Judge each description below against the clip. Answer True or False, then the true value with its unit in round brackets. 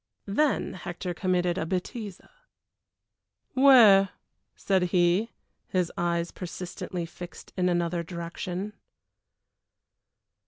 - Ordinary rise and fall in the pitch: False (2.1 semitones)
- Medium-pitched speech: True (180 Hz)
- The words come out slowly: True (85 wpm)